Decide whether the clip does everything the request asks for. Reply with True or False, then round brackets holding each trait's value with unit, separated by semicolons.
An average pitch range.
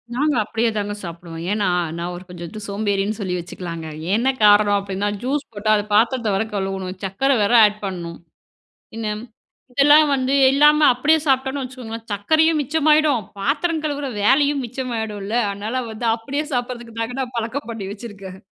True (5.0 semitones)